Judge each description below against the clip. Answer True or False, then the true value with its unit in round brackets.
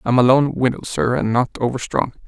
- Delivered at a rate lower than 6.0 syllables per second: True (5.5 syllables/s)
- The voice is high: False (125 Hz)